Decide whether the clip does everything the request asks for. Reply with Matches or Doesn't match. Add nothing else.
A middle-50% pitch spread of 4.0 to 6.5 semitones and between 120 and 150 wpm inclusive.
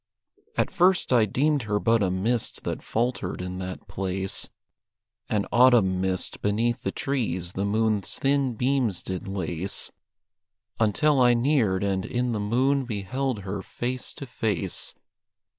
Matches